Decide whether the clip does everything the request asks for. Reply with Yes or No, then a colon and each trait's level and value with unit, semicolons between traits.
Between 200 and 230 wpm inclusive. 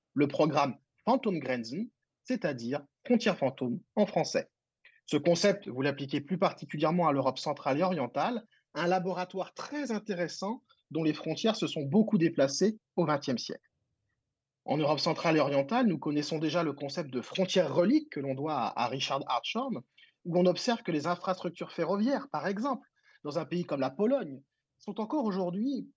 No: average, 165 wpm